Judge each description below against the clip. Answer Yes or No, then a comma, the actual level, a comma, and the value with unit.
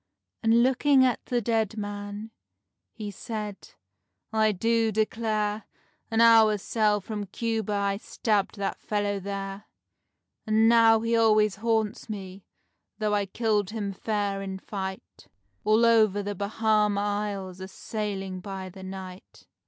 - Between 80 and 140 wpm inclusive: Yes, slow, 135 wpm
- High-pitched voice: Yes, high, 210 Hz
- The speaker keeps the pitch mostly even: Yes, narrow, 2.0 semitones